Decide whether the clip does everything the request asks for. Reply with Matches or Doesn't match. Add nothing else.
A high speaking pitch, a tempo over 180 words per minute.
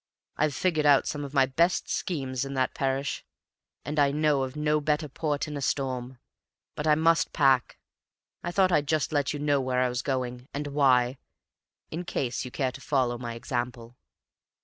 Doesn't match